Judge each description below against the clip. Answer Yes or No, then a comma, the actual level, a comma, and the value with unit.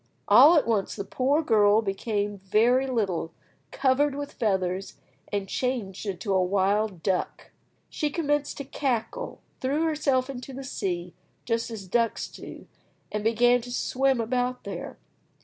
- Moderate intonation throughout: Yes, average, 5.0 semitones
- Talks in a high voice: Yes, high, 230 Hz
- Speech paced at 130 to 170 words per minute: Yes, average, 145 wpm